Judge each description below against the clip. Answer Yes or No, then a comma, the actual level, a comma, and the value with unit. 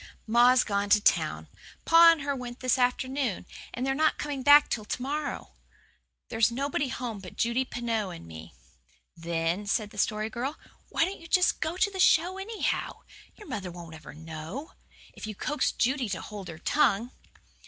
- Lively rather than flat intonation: Yes, wide, 6.1 semitones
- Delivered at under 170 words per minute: No, average, 180 wpm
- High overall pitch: Yes, high, 245 Hz